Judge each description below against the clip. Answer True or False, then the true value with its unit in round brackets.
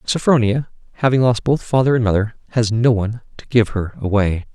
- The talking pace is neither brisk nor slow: True (185 wpm)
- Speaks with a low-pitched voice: True (115 Hz)